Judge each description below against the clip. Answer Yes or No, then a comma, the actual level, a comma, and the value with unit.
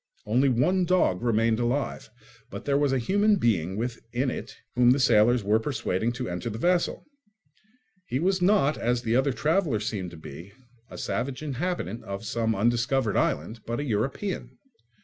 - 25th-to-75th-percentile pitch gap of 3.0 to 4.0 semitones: No, average, 4.4 semitones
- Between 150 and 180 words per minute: Yes, average, 170 wpm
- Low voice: Yes, low, 120 Hz